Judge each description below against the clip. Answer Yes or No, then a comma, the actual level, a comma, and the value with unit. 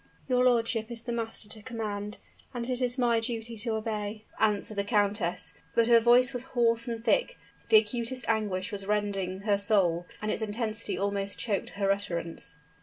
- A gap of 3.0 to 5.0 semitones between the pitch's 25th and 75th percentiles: No, narrow, 2.5 semitones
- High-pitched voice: Yes, high, 220 Hz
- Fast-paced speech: No, average, 180 wpm